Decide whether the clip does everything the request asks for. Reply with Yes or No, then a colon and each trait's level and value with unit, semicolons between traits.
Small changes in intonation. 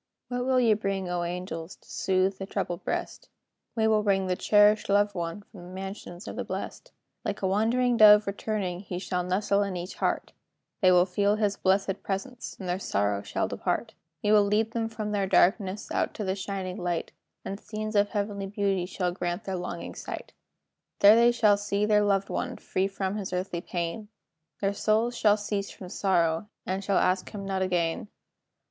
Yes: narrow, 2.3 semitones